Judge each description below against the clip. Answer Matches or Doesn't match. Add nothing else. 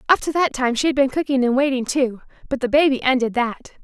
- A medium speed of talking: Doesn't match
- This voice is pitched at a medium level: Doesn't match